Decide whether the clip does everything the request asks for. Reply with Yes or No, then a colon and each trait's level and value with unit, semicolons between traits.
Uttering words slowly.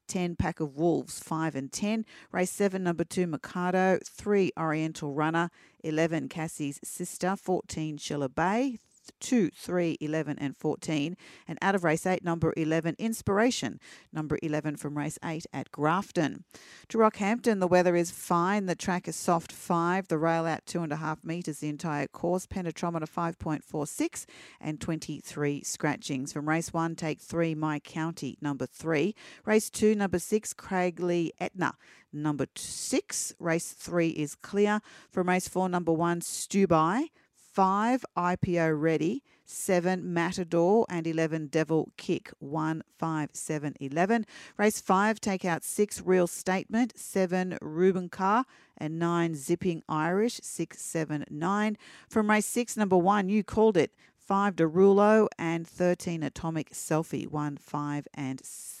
No: average, 145 wpm